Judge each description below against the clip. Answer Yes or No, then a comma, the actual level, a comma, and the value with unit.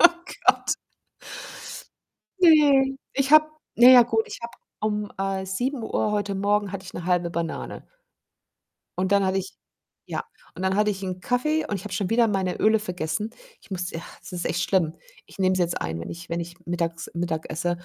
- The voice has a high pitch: Yes, high, 195 Hz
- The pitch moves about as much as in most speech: Yes, average, 3.9 semitones